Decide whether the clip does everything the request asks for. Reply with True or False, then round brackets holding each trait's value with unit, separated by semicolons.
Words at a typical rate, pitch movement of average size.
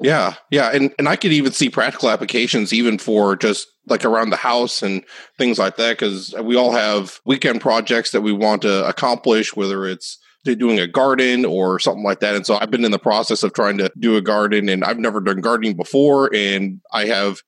False (215 wpm; 3.5 semitones)